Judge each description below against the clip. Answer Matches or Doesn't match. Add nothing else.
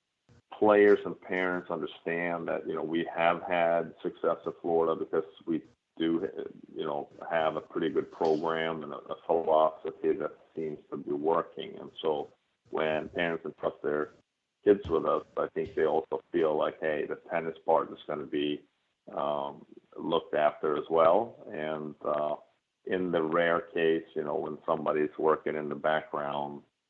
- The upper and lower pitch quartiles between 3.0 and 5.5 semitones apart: Doesn't match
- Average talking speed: Matches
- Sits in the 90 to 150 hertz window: Doesn't match